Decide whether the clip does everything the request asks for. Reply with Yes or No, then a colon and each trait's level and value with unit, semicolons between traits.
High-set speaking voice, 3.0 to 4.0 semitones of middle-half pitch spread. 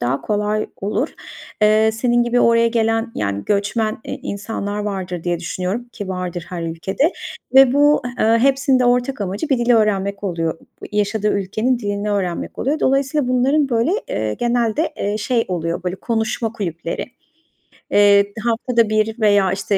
Yes: high, 215 Hz; average, 3.7 semitones